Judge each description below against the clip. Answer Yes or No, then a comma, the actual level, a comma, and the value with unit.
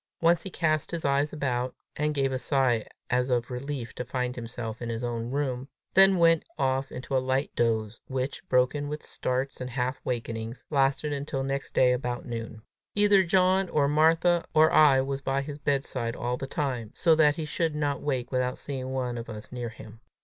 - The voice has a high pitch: No, low, 135 Hz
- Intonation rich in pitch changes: No, average, 3.2 semitones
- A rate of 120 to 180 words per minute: No, average, 195 wpm